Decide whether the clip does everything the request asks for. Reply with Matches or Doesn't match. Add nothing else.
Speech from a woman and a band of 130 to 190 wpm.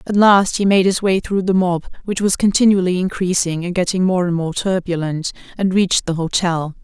Doesn't match